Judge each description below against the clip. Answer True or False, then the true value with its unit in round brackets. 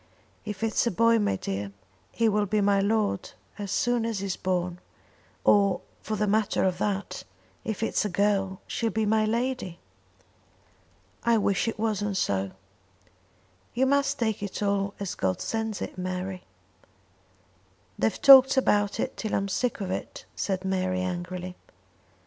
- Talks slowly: False (155 wpm)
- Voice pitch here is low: False (200 Hz)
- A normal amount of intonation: True (3.1 semitones)